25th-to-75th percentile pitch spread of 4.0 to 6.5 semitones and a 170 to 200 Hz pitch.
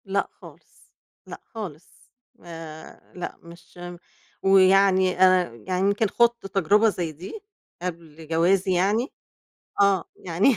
No: average, 2.7 semitones; medium, 185 Hz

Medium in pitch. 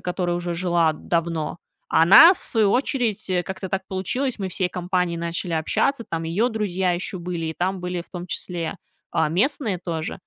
Yes: medium, 180 Hz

